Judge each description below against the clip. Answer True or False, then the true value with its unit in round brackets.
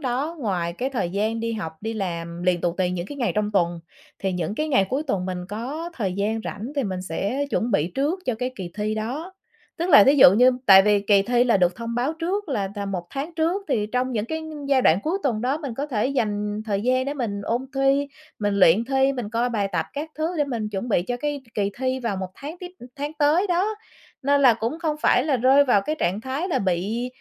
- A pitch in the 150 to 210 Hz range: False (235 Hz)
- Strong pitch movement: True (5.7 semitones)